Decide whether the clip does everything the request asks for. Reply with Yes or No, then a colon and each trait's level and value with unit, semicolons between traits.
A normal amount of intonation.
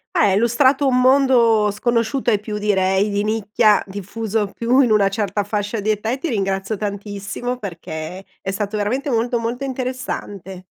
Yes: average, 3.2 semitones